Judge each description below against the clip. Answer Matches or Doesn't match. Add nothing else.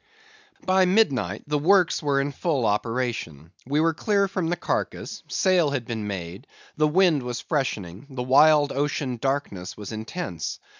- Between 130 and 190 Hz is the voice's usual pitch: Matches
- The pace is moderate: Matches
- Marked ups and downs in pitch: Matches